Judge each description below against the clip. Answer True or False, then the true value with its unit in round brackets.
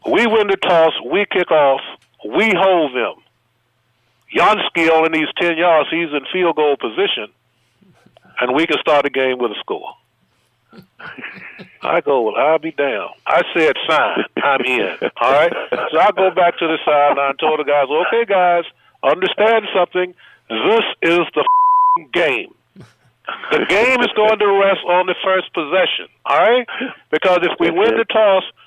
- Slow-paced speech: False (165 wpm)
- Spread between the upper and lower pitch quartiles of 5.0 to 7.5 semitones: True (5.6 semitones)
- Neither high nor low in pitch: True (180 Hz)